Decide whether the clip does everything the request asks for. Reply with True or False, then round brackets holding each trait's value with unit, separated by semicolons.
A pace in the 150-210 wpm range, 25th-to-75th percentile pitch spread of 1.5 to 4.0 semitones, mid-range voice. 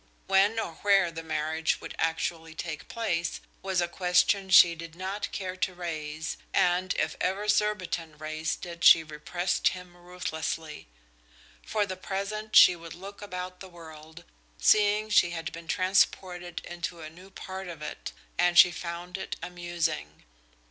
True (155 wpm; 2.6 semitones; 175 Hz)